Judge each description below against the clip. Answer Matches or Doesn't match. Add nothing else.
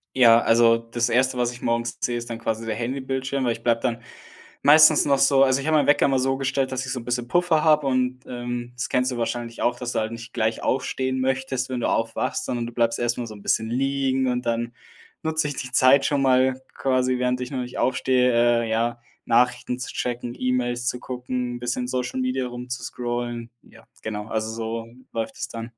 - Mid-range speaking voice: Doesn't match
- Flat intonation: Matches